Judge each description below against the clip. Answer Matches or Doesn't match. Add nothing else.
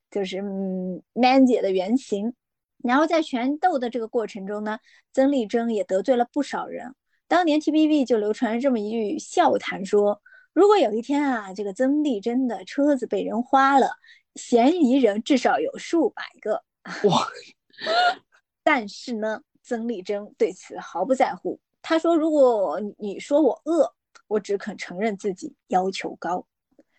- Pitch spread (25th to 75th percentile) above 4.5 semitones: Matches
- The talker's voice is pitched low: Doesn't match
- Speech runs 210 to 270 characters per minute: Matches